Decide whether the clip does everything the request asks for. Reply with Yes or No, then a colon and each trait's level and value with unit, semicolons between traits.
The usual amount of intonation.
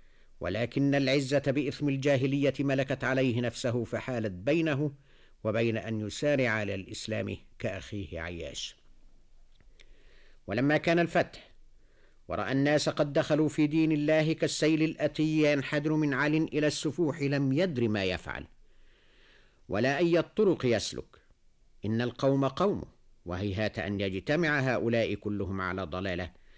No: wide, 6.3 semitones